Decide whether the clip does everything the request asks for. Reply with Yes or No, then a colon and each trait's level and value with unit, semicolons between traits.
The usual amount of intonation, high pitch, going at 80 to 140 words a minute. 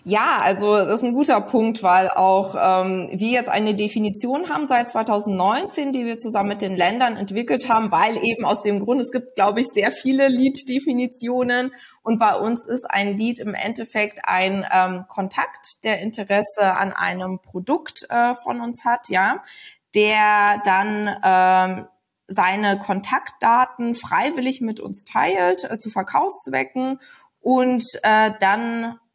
No: average, 3.8 semitones; high, 220 Hz; average, 150 wpm